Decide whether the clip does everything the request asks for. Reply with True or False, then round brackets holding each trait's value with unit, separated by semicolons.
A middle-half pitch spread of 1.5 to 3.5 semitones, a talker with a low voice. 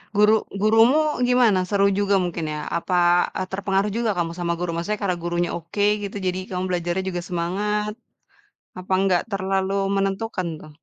False (2.8 semitones; 190 Hz)